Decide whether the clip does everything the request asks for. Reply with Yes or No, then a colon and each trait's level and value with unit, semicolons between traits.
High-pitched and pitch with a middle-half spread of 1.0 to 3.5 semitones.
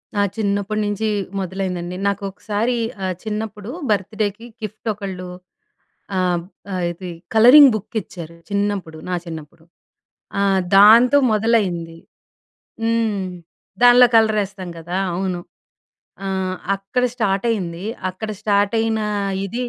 Yes: high, 200 Hz; average, 2.9 semitones